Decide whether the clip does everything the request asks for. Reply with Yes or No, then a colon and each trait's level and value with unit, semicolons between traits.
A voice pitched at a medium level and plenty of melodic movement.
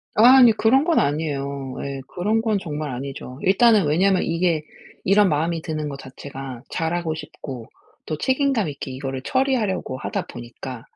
Yes: medium, 155 Hz; wide, 6.9 semitones